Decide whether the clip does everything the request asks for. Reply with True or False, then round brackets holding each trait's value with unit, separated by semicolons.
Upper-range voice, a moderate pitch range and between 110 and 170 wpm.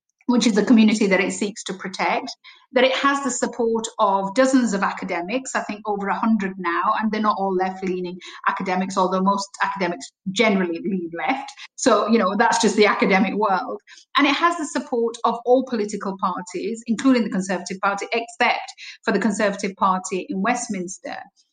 False (215 Hz; 3.9 semitones; 180 wpm)